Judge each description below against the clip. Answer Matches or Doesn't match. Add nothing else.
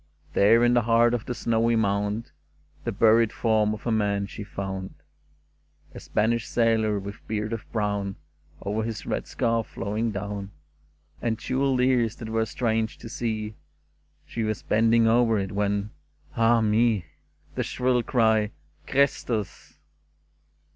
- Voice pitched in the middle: Doesn't match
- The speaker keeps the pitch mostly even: Matches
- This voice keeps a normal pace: Matches